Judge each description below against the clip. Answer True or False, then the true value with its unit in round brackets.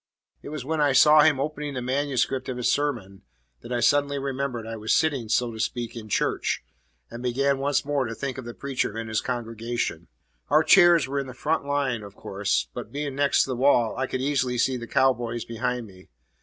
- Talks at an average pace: False (215 wpm)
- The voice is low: True (130 Hz)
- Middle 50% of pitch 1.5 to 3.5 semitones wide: True (3.2 semitones)